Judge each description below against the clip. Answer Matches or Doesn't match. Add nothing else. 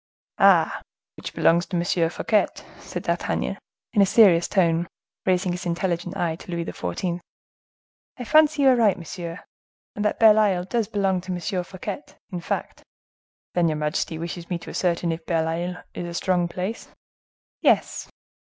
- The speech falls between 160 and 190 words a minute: Matches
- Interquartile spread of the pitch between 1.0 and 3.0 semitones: Matches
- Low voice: Doesn't match